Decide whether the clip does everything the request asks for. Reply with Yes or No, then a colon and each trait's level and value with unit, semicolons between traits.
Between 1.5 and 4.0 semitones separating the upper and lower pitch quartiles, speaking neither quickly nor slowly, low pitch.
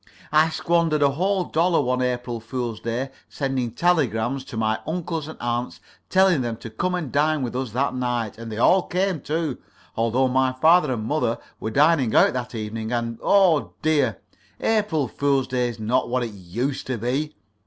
No: average, 4.8 semitones; average, 185 wpm; low, 130 Hz